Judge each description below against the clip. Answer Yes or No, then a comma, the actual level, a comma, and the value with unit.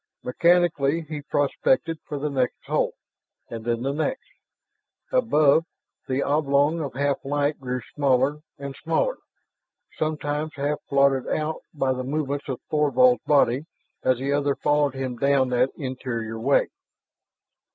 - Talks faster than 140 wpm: No, slow, 135 wpm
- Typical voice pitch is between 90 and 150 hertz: Yes, medium, 140 Hz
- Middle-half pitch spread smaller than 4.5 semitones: Yes, narrow, 2.4 semitones